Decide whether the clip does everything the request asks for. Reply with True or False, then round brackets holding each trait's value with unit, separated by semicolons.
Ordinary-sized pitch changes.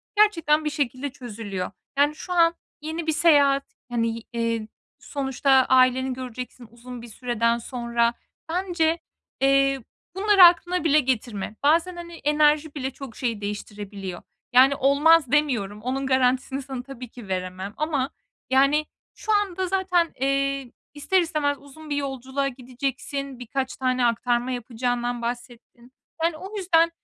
True (4.1 semitones)